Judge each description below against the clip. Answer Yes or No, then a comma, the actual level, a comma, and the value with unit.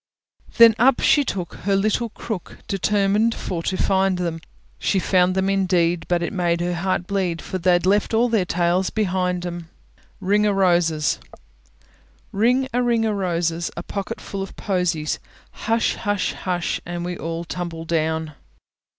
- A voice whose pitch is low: No, medium, 185 Hz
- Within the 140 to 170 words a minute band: Yes, average, 160 wpm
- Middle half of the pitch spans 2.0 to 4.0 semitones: Yes, average, 2.8 semitones